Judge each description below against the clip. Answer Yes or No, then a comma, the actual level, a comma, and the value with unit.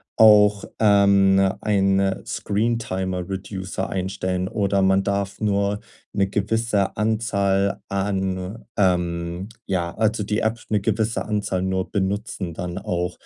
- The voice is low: Yes, low, 100 Hz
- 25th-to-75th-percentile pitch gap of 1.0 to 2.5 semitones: Yes, narrow, 1.8 semitones